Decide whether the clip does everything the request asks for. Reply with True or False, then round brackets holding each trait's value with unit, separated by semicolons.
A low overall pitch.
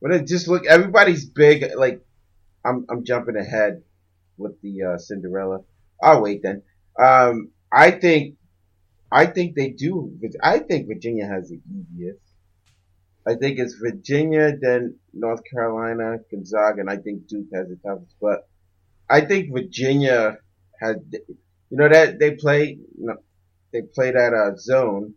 True (115 Hz)